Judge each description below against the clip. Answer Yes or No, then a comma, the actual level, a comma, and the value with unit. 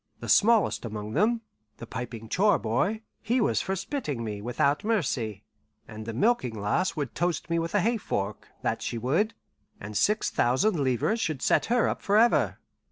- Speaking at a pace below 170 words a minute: No, average, 175 wpm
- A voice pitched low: No, medium, 155 Hz